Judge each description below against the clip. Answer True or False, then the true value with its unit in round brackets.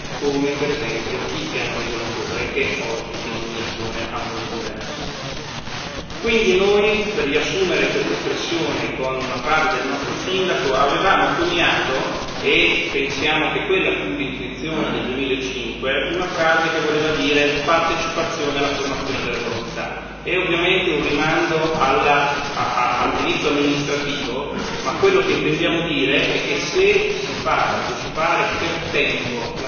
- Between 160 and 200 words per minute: False (125 wpm)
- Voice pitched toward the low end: False (145 Hz)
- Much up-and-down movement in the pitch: False (5.0 semitones)